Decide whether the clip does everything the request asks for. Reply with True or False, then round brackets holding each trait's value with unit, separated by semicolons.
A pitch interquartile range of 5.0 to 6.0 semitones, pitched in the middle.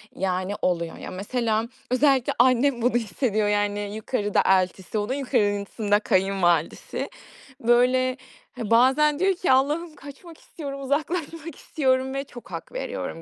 False (5.3 semitones; 245 Hz)